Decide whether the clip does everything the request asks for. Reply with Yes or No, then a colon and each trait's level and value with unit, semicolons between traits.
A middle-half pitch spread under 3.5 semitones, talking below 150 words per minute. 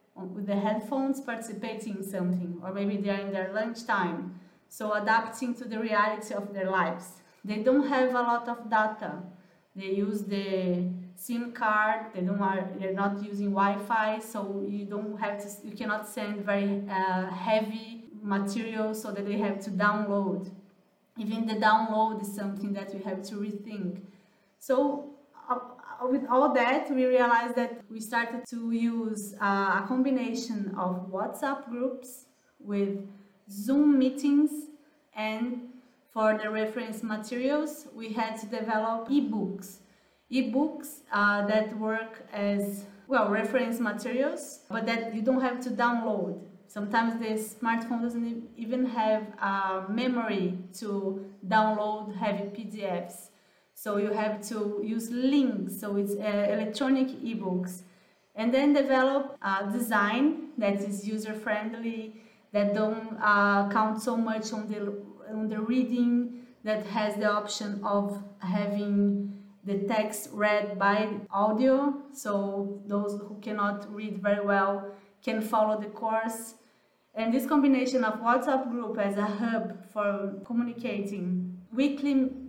Yes: average, 2.9 semitones; average, 140 wpm